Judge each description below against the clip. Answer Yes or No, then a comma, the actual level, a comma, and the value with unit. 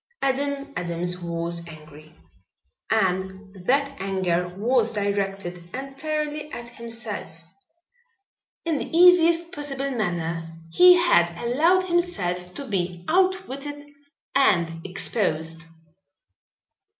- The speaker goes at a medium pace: No, slow, 90 wpm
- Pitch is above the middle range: Yes, high, 220 Hz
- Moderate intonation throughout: No, wide, 8.5 semitones